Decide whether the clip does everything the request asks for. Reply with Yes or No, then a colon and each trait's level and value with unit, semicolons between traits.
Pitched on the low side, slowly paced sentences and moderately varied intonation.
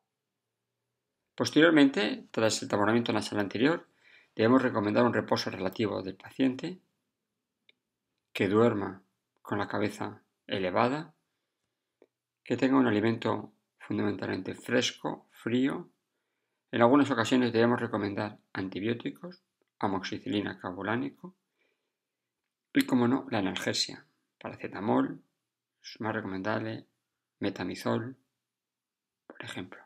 Yes: low, 115 Hz; slow, 95 wpm; average, 4.2 semitones